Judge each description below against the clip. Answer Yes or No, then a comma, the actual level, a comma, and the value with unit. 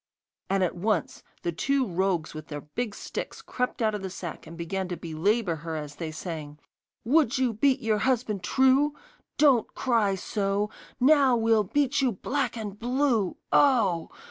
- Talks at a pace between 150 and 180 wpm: Yes, average, 170 wpm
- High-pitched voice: Yes, high, 210 Hz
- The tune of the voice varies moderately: No, wide, 6.6 semitones